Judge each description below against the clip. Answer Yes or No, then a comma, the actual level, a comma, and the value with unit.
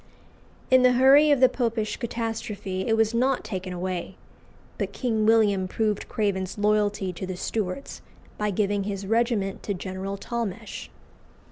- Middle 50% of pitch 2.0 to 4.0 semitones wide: Yes, average, 3.3 semitones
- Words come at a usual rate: Yes, average, 145 wpm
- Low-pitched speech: No, high, 210 Hz